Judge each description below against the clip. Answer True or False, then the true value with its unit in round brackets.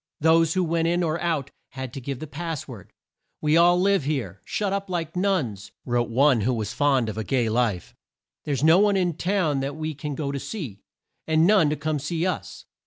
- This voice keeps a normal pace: False (220 wpm)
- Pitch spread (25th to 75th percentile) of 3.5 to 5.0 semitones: True (4.7 semitones)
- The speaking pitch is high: False (150 Hz)